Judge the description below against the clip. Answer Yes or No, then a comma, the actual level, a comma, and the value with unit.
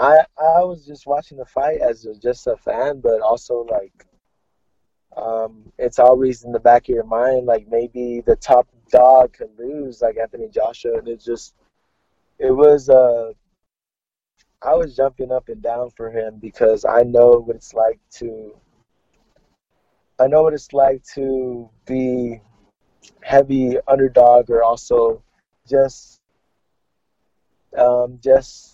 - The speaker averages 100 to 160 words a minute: Yes, average, 145 wpm